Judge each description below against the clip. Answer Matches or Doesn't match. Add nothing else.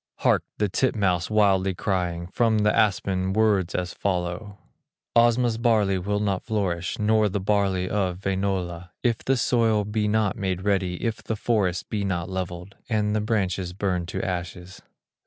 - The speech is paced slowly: Doesn't match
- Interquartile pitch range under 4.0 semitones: Matches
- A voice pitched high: Doesn't match